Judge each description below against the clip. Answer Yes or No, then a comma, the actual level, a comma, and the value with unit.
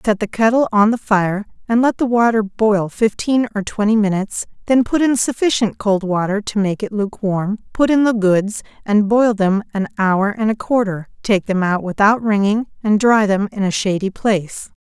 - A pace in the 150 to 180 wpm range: No, average, 195 wpm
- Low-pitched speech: No, high, 210 Hz